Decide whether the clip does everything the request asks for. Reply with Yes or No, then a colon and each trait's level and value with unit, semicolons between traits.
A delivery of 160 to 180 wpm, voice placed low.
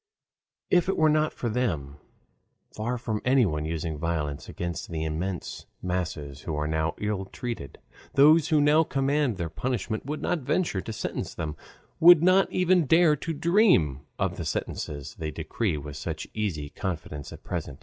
Yes: average, 165 wpm; low, 105 Hz